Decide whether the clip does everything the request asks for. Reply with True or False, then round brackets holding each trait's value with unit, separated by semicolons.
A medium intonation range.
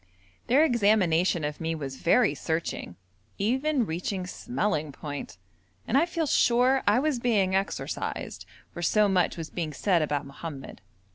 False (7.2 semitones)